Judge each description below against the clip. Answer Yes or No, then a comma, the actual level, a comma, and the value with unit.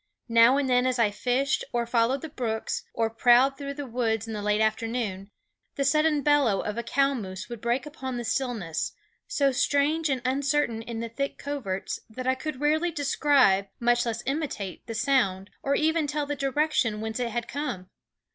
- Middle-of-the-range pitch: No, very high, 250 Hz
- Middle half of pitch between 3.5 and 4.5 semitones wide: Yes, average, 3.8 semitones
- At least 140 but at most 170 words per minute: No, average, 190 wpm